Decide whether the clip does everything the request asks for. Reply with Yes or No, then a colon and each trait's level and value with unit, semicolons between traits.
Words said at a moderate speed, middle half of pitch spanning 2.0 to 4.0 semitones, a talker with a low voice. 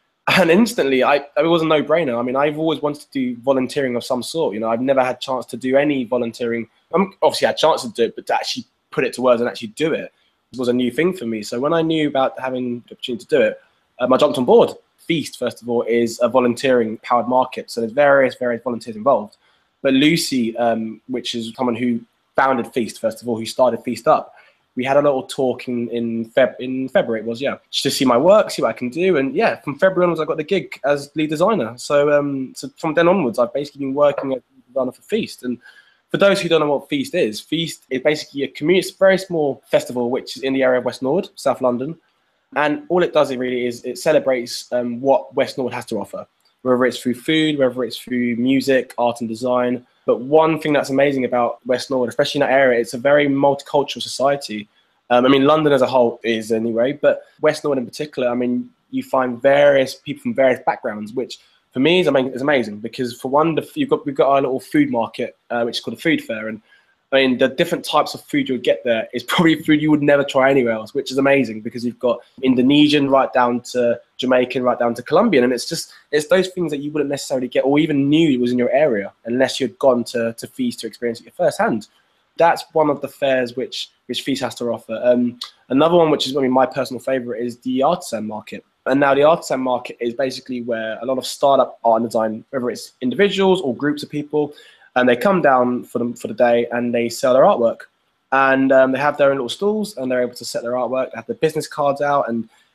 No: fast, 245 wpm; average, 3.4 semitones; low, 130 Hz